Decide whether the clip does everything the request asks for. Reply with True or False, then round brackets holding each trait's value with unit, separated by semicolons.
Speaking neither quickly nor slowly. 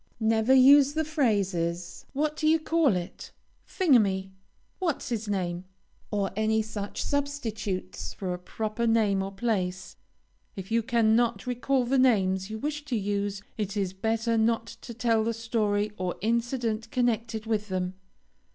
True (150 wpm)